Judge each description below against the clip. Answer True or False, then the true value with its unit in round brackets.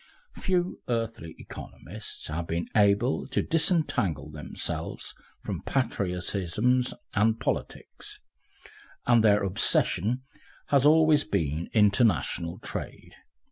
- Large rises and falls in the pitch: True (6.8 semitones)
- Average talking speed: False (95 wpm)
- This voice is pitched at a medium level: False (110 Hz)